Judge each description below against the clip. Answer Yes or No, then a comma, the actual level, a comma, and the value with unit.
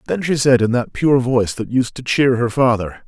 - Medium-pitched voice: No, low, 120 Hz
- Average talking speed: No, fast, 255 wpm